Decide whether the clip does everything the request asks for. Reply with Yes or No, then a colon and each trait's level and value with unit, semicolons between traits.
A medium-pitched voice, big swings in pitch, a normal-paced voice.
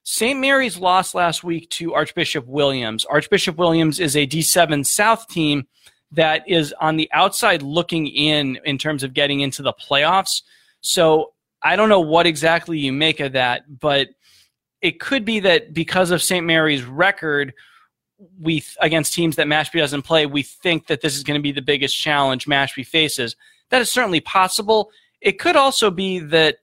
No: medium, 160 Hz; average, 4.0 semitones; average, 175 wpm